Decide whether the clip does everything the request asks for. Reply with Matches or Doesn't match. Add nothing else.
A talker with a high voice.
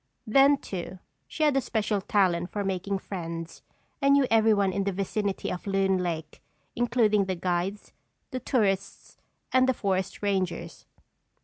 Matches